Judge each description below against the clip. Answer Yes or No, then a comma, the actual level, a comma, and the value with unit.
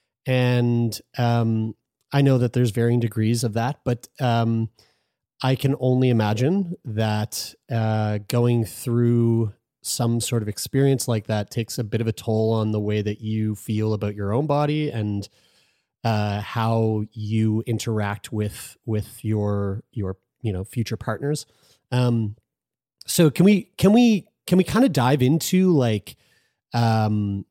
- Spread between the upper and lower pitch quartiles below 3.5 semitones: Yes, average, 2.9 semitones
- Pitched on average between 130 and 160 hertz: No, low, 115 Hz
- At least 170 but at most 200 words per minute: No, average, 150 wpm